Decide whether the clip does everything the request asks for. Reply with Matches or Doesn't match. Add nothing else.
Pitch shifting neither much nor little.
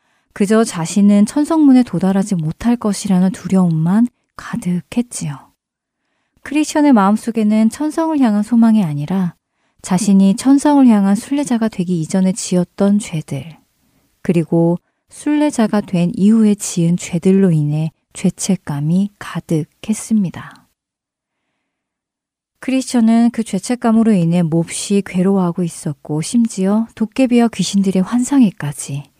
Matches